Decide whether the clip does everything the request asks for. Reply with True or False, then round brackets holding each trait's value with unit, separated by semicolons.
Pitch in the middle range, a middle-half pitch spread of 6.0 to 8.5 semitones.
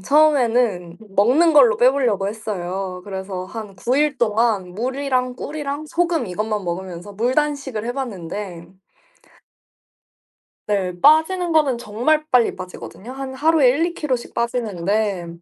False (235 Hz; 6.3 semitones)